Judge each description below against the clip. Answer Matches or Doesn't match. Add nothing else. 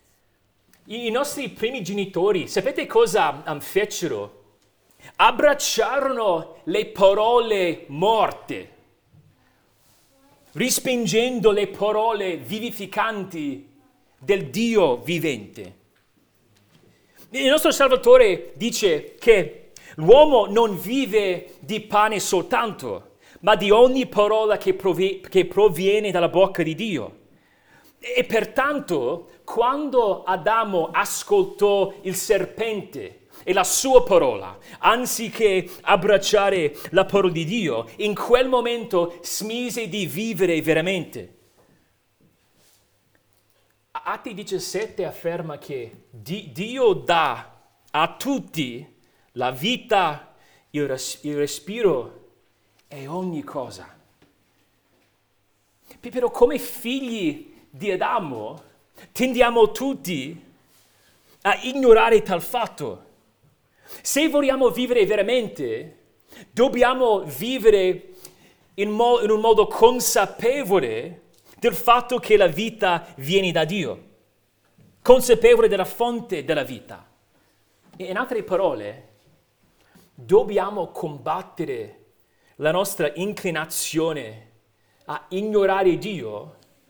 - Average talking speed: Doesn't match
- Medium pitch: Doesn't match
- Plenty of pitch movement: Matches